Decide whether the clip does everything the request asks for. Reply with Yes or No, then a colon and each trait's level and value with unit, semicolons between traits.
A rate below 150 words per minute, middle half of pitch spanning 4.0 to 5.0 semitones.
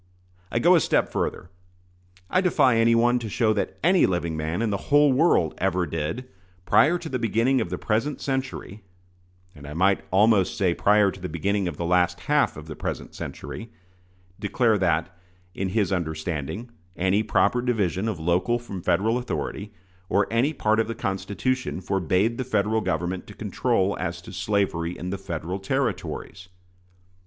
No: average, 170 wpm; average, 4.7 semitones